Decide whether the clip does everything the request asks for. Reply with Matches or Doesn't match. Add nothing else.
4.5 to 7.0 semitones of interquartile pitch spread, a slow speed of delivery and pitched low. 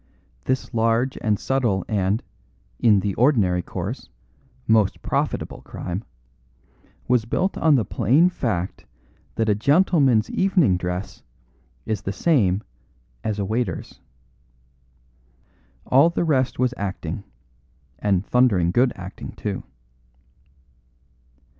Matches